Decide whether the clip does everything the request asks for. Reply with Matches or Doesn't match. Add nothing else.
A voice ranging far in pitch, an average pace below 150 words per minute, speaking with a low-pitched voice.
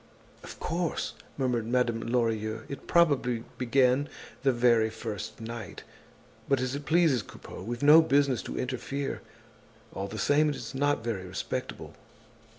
Doesn't match